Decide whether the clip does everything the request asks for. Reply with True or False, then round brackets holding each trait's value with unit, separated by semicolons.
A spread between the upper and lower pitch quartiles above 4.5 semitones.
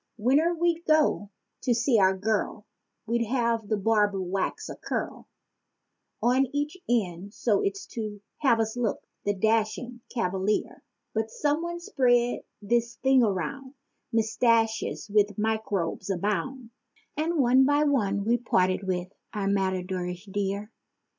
False (4.1 semitones)